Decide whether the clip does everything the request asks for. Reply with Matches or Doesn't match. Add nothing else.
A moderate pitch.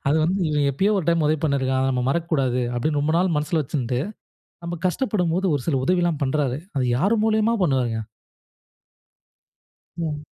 Matches